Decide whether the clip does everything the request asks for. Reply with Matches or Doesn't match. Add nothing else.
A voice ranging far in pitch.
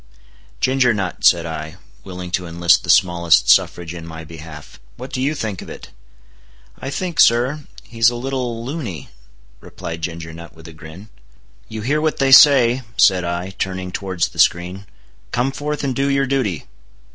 Matches